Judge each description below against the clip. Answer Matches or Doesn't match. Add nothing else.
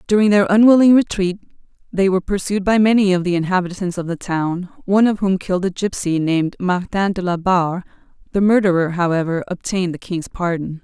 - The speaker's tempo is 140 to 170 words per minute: Doesn't match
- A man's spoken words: Doesn't match